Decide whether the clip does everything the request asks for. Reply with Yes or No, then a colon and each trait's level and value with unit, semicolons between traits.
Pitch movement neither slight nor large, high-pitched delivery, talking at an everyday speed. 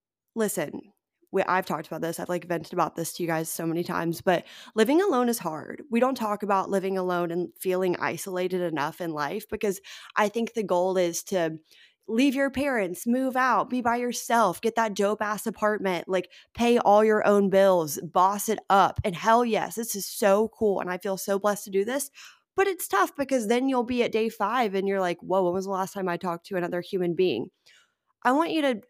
No: average, 4.4 semitones; high, 200 Hz; fast, 220 wpm